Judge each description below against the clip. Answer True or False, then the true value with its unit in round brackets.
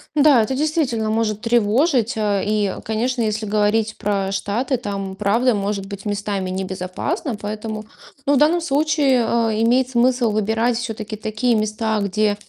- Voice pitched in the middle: False (220 Hz)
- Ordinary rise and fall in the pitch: True (3.1 semitones)